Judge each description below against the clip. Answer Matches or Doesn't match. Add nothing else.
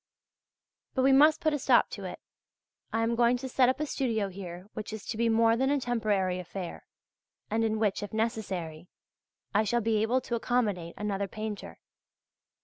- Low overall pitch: Doesn't match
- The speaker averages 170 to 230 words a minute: Matches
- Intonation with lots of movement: Doesn't match